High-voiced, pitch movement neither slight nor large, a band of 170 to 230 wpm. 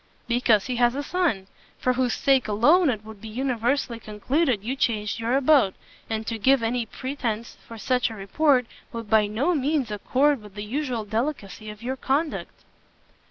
Yes: high, 240 Hz; average, 4.0 semitones; average, 175 wpm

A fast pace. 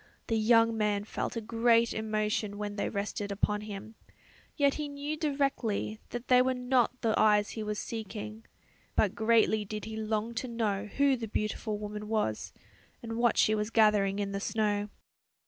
No: average, 175 wpm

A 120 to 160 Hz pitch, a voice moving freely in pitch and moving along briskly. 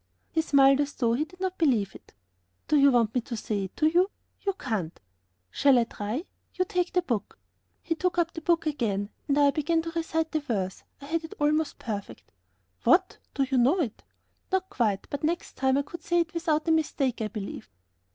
No: very high, 290 Hz; wide, 5.7 semitones; fast, 210 wpm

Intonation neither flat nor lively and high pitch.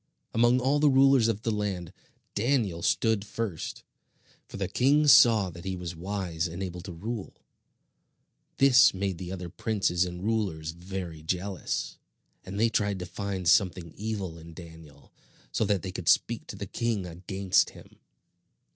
No: average, 4.1 semitones; very low, 95 Hz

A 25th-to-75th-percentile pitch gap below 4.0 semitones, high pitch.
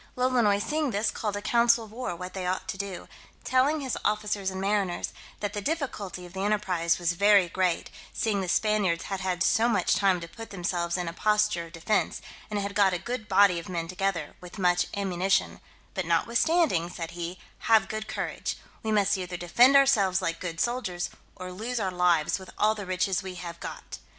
Yes: average, 3.2 semitones; high, 195 Hz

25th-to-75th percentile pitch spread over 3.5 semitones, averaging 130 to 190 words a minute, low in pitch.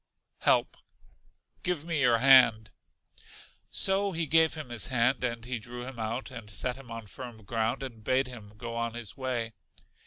No: average, 2.7 semitones; average, 175 wpm; low, 120 Hz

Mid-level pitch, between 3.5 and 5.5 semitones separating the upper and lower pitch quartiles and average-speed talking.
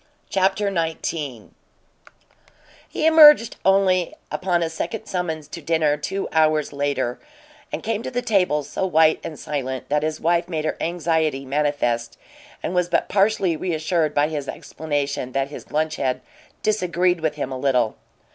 Yes: medium, 160 Hz; average, 3.8 semitones; average, 155 wpm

